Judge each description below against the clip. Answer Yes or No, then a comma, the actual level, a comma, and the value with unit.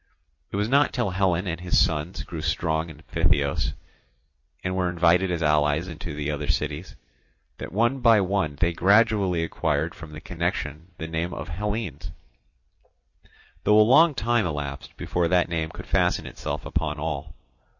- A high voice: No, very low, 85 Hz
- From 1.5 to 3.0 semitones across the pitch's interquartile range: No, average, 4.0 semitones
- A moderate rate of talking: Yes, average, 160 wpm